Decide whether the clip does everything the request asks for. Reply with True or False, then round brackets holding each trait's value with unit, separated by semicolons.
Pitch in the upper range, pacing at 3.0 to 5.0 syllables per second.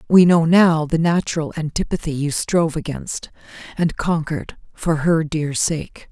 False (160 Hz; 4.5 syllables/s)